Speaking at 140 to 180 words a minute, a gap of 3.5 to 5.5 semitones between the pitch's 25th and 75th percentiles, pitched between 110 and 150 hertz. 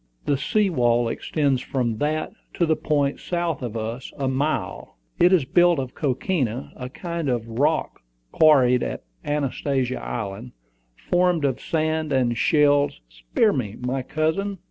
Yes: average, 145 wpm; average, 4.3 semitones; medium, 140 Hz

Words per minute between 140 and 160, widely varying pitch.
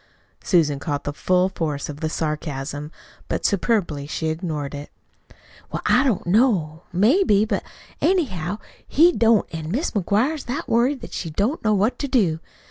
Yes: average, 155 wpm; wide, 7.1 semitones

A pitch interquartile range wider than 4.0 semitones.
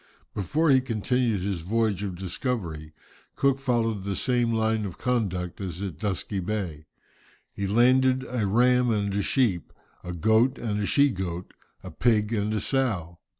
Yes: average, 4.7 semitones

